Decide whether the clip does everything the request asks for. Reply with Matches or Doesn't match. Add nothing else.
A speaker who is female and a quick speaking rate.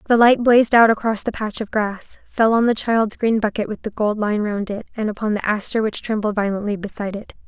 Matches